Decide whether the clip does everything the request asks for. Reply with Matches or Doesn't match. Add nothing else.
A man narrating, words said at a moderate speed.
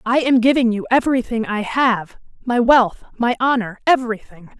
Doesn't match